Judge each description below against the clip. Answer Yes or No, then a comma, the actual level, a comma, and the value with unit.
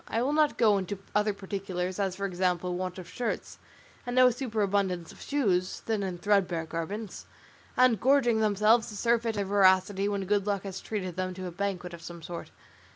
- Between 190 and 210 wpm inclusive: Yes, average, 195 wpm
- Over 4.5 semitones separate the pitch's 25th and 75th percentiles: No, average, 3.1 semitones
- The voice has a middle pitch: No, high, 200 Hz